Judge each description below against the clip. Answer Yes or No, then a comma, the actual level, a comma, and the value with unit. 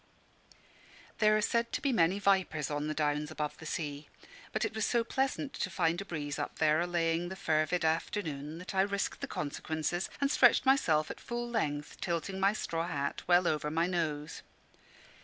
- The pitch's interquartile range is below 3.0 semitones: No, average, 4.6 semitones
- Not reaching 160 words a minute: No, average, 185 wpm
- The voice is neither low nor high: Yes, medium, 170 Hz